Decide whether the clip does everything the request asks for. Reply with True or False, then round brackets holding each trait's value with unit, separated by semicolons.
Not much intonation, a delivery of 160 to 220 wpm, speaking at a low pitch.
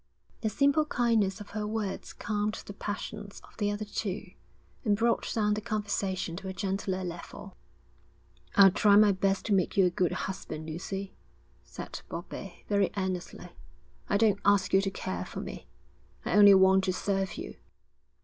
False (1.8 semitones; 170 wpm; 200 Hz)